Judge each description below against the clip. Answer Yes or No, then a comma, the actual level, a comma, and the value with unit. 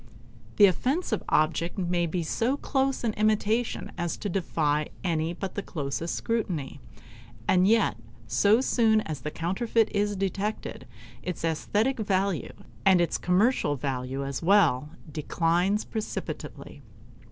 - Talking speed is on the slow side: Yes, slow, 130 wpm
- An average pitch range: Yes, average, 5.0 semitones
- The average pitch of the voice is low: No, medium, 185 Hz